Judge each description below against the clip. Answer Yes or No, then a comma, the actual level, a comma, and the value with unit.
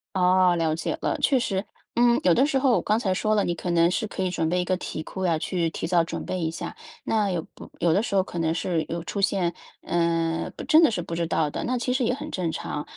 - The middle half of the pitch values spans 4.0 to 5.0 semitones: Yes, average, 4.3 semitones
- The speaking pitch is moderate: Yes, medium, 180 Hz